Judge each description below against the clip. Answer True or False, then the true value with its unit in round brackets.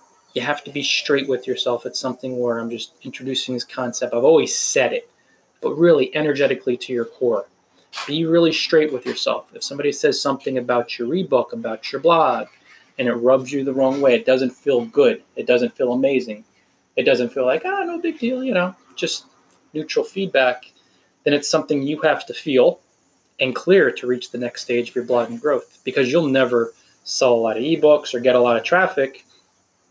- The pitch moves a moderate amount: True (4.4 semitones)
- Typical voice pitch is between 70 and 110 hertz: False (135 Hz)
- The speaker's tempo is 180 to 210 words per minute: True (205 wpm)